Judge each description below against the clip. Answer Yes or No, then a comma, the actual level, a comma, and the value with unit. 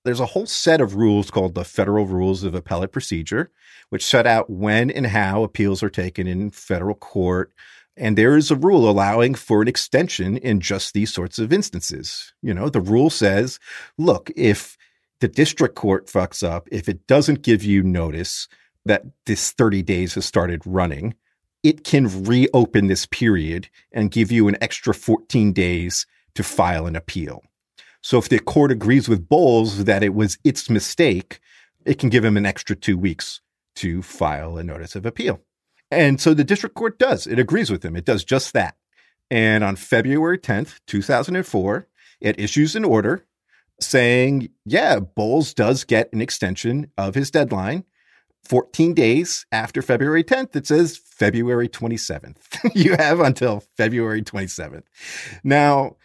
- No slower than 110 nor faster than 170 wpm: Yes, average, 165 wpm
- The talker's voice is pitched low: Yes, low, 110 Hz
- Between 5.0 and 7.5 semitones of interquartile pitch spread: Yes, wide, 5.5 semitones